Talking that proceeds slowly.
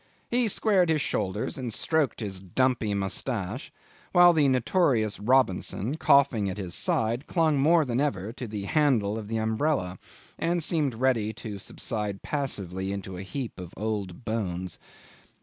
No: average, 150 wpm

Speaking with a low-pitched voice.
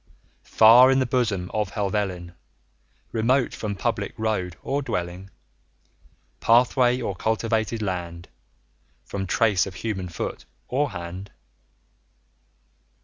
Yes: low, 105 Hz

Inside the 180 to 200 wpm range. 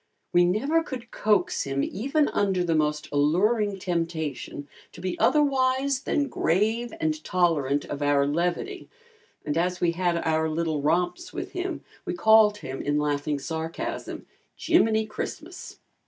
No: average, 140 wpm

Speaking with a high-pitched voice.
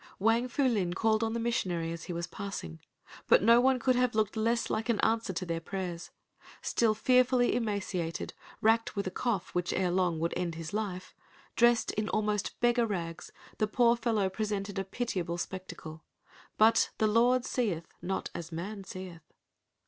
Yes: high, 210 Hz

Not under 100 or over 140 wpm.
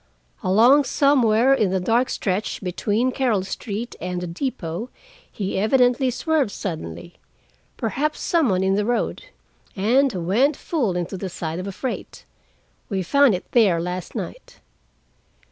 Yes: slow, 135 wpm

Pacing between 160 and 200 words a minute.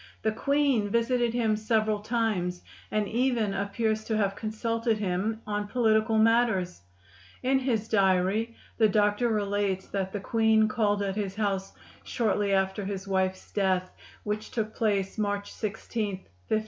No: average, 145 wpm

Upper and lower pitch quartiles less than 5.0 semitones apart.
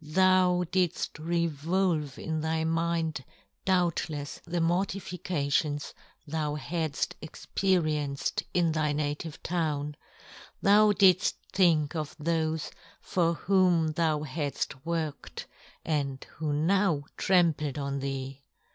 Yes: average, 2.9 semitones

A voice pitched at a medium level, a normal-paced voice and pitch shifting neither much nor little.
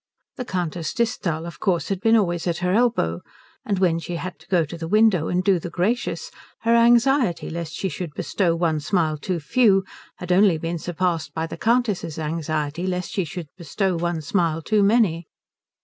Yes: medium, 175 Hz; average, 190 wpm; average, 3.5 semitones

